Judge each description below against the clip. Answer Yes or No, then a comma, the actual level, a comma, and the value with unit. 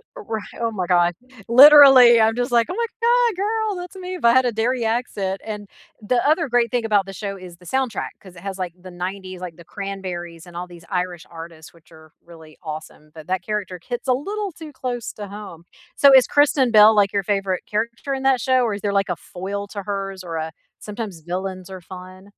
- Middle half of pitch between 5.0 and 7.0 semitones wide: Yes, average, 5.3 semitones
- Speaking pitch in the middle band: No, high, 200 Hz